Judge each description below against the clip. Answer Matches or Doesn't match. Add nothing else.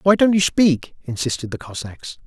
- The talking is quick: Doesn't match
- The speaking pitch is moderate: Matches